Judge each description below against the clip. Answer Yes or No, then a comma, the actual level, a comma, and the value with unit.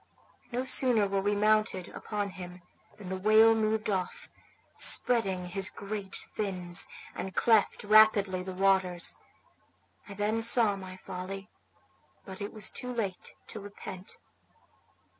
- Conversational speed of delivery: No, slow, 130 wpm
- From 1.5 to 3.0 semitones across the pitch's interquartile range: Yes, narrow, 2.5 semitones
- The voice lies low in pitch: No, high, 200 Hz